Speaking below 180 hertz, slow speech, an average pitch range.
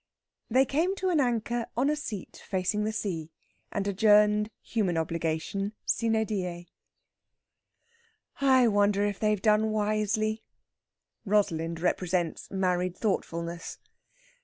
No: high, 210 Hz; slow, 110 wpm; average, 3.4 semitones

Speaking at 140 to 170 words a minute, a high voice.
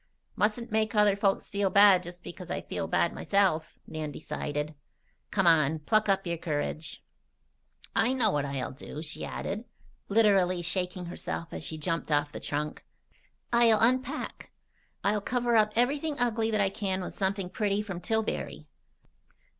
Yes: average, 155 wpm; high, 195 Hz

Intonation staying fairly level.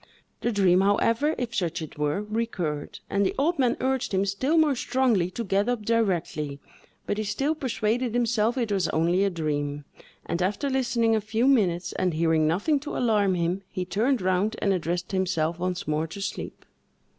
No: average, 5.1 semitones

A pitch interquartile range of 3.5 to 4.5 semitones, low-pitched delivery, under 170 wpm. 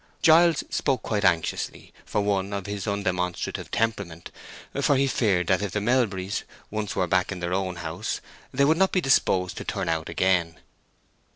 No: average, 3.9 semitones; low, 100 Hz; average, 175 wpm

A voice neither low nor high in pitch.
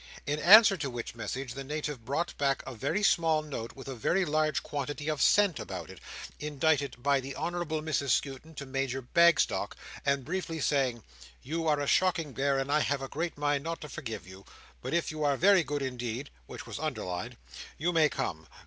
Yes: medium, 145 Hz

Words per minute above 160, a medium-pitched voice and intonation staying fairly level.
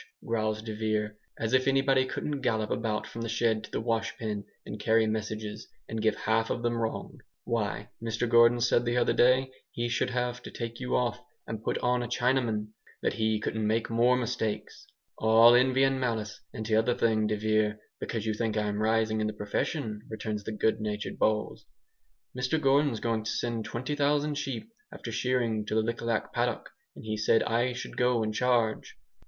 No: average, 190 wpm; low, 115 Hz; narrow, 2.2 semitones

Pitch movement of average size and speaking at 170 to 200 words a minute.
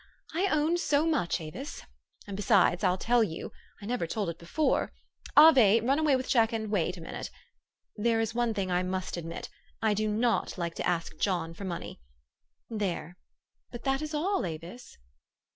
No: wide, 6.4 semitones; average, 175 wpm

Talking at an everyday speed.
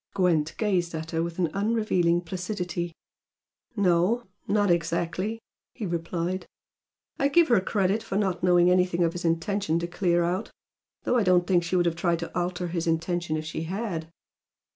Yes: average, 170 wpm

